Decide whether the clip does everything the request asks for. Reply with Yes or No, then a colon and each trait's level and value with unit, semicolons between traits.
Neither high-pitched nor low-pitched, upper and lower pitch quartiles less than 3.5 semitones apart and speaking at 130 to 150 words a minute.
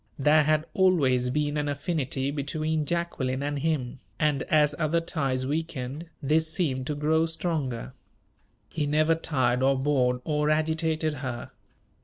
Yes: medium, 150 Hz; average, 3.0 semitones; average, 140 wpm